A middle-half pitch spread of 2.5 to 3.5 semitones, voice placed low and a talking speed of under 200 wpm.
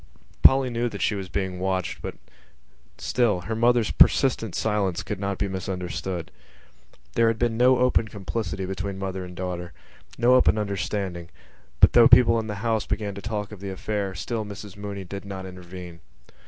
Yes: average, 3.0 semitones; low, 100 Hz; average, 175 wpm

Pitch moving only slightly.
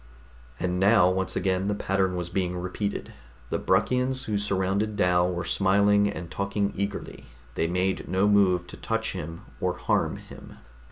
Yes: narrow, 2.1 semitones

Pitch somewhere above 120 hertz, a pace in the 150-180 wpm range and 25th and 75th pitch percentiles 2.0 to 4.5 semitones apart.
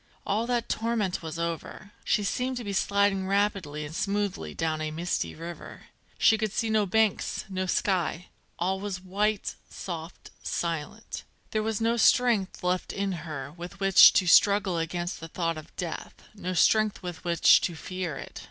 Yes: medium, 185 Hz; average, 170 wpm; average, 3.5 semitones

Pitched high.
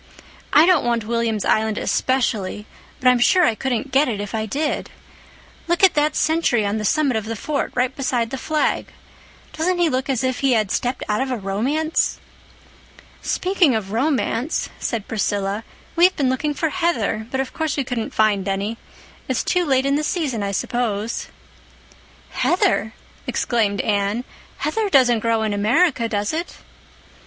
Yes: high, 245 Hz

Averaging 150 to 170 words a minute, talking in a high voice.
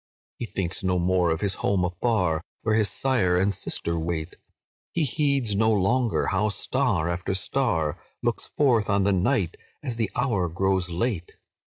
No: average, 165 wpm; very low, 95 Hz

